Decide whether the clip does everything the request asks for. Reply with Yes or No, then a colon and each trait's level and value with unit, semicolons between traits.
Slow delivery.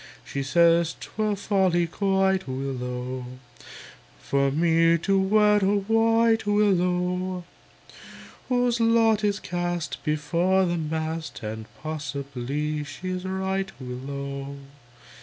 Yes: slow, 100 wpm